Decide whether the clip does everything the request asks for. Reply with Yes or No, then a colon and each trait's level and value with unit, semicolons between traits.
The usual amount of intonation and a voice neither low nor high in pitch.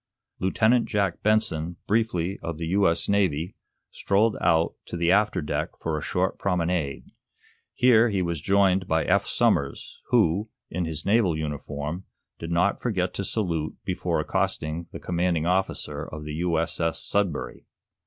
No: average, 3.7 semitones; very low, 90 Hz